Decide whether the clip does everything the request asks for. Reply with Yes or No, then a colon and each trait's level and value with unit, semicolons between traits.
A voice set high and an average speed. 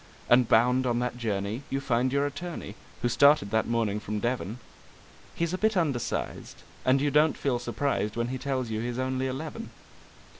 No: low, 125 Hz; average, 180 wpm